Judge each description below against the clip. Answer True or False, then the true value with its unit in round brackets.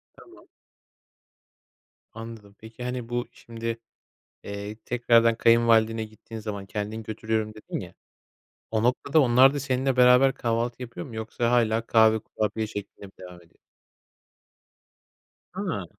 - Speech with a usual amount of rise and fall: False (1.9 semitones)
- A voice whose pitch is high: False (115 Hz)